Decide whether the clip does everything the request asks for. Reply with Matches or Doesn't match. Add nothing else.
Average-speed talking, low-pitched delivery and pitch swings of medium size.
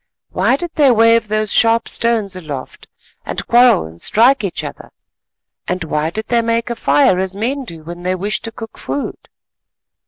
Doesn't match